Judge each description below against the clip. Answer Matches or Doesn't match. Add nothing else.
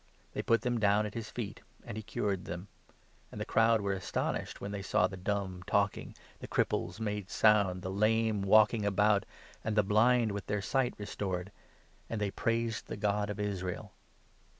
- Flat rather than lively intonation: Matches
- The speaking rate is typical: Matches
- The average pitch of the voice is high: Doesn't match